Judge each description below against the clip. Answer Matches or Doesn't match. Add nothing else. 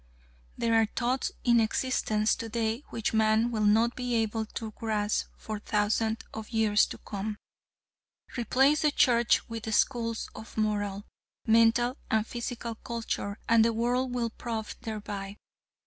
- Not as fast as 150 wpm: Matches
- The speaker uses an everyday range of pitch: Doesn't match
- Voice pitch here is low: Doesn't match